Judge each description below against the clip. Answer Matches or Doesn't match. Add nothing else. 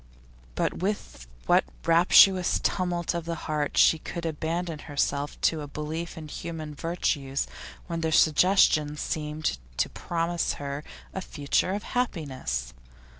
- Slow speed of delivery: Matches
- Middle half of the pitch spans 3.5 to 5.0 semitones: Doesn't match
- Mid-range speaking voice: Matches